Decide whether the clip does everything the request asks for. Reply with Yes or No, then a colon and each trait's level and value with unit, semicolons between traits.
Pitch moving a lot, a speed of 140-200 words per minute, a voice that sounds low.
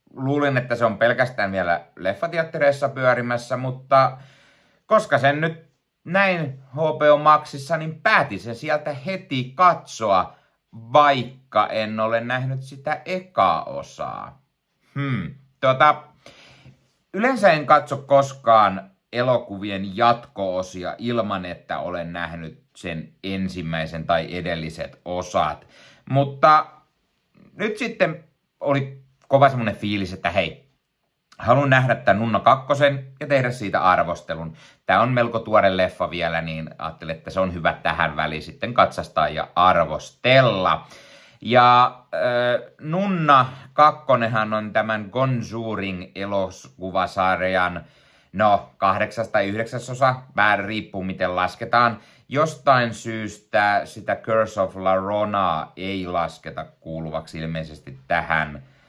No: wide, 6.8 semitones; average, 110 wpm; low, 120 Hz